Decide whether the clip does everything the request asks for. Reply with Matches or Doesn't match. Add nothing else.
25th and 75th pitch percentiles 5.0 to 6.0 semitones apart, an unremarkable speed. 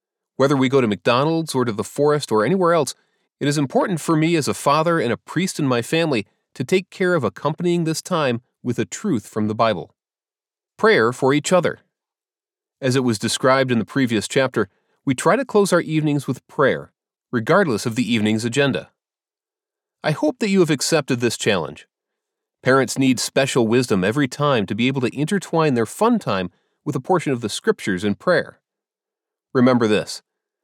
Matches